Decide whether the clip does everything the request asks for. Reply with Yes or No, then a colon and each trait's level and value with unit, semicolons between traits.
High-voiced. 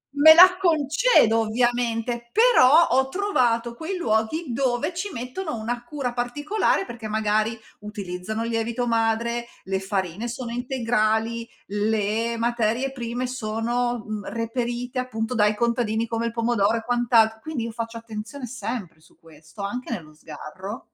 Yes: high, 235 Hz